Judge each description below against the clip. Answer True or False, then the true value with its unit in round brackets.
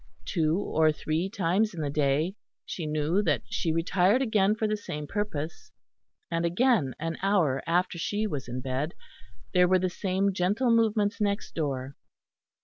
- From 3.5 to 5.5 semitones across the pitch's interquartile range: True (4.9 semitones)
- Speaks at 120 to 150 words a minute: False (160 wpm)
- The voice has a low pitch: False (175 Hz)